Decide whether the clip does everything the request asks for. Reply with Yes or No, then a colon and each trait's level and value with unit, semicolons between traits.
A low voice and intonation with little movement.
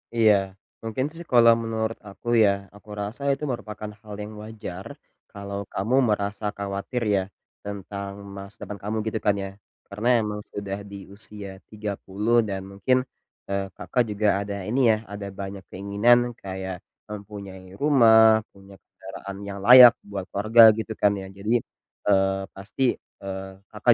Yes: low, 100 Hz; narrow, 2.1 semitones